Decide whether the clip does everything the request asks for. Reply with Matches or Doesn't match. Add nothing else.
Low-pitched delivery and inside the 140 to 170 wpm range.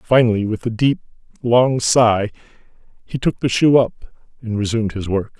Matches